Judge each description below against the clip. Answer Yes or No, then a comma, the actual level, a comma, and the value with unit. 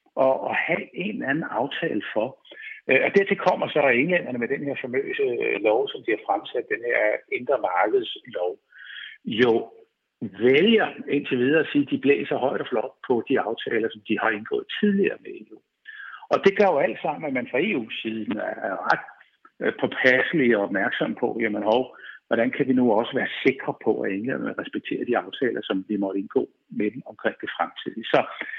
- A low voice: No, very high, 290 Hz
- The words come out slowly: No, average, 190 wpm